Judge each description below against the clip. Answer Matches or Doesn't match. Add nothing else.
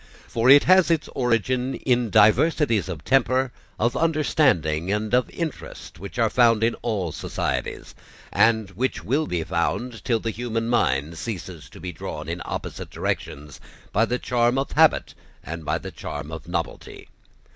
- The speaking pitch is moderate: Doesn't match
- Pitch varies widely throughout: Matches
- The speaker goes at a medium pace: Matches